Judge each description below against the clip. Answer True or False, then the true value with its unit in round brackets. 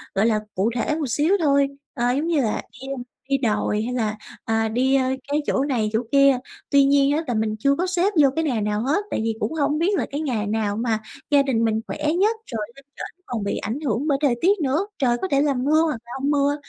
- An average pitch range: True (4.7 semitones)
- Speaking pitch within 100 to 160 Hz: False (270 Hz)